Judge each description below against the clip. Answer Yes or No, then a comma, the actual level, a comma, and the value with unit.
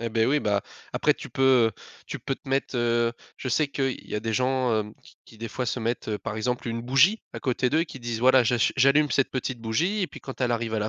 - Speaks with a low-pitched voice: Yes, low, 125 Hz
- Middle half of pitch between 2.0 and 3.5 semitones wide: Yes, average, 2.7 semitones